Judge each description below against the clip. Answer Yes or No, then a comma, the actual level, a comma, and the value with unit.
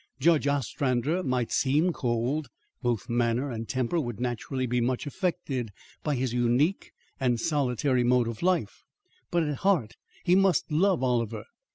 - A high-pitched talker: No, low, 130 Hz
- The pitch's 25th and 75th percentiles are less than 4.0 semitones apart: No, average, 4.3 semitones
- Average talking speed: Yes, average, 150 wpm